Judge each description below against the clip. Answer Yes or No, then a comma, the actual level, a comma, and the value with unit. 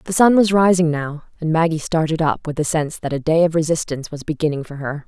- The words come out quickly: Yes, fast, 250 wpm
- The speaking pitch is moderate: Yes, medium, 160 Hz